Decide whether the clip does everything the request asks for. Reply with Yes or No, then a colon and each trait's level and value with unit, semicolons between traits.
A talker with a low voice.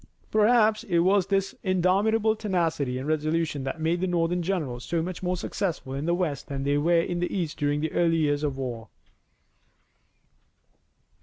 No: medium, 170 Hz